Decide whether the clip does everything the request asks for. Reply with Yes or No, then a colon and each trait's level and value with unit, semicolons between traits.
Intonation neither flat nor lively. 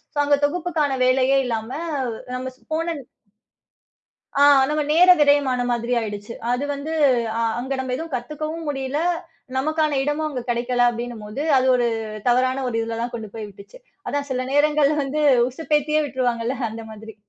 Yes: average, 3.8 semitones